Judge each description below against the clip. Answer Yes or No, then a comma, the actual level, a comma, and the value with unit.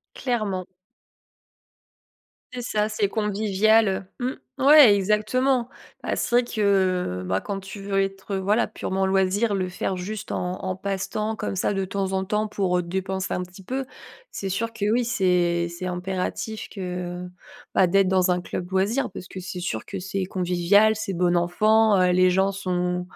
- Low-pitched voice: No, high, 195 Hz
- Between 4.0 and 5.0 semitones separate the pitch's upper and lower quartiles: No, average, 2.7 semitones